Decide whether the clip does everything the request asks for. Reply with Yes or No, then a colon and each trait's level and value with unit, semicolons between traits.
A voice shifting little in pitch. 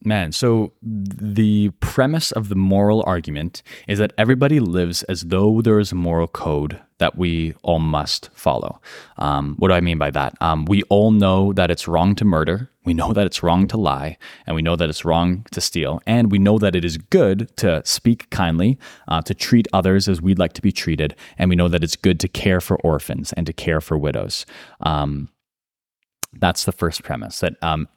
No: average, 4.0 semitones